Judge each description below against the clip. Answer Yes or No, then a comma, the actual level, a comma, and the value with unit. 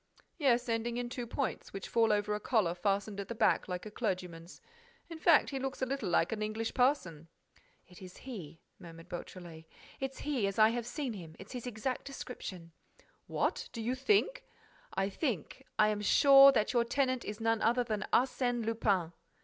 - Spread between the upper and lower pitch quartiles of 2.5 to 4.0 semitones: No, average, 4.7 semitones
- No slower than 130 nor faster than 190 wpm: Yes, average, 185 wpm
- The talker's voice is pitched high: Yes, high, 225 Hz